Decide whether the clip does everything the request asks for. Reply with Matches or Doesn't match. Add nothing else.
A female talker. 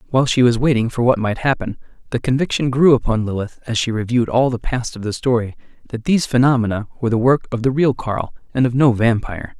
Doesn't match